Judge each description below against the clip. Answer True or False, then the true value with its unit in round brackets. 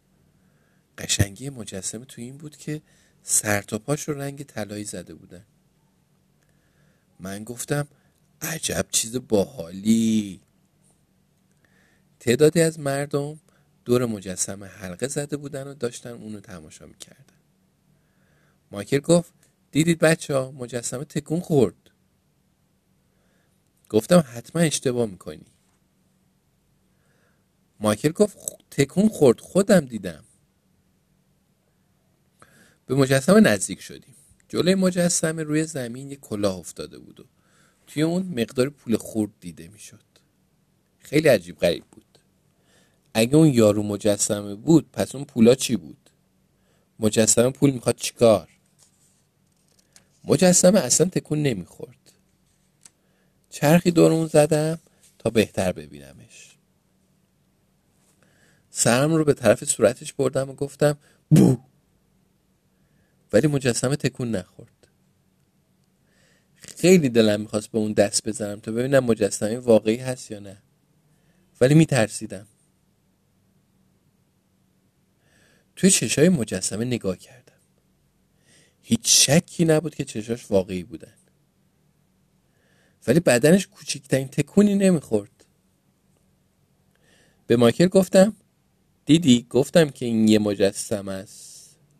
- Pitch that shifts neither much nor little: False (6.2 semitones)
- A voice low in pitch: True (130 Hz)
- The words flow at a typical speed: False (100 wpm)